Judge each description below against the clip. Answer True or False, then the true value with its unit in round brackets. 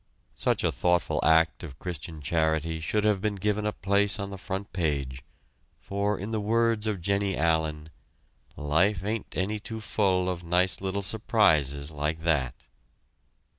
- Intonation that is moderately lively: True (4.3 semitones)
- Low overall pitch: True (90 Hz)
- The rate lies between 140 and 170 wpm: True (155 wpm)